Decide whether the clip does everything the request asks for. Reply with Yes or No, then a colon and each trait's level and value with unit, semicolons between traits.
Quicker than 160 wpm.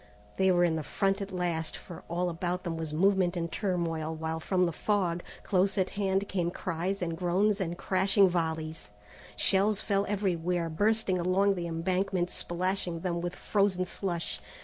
Yes: average, 170 wpm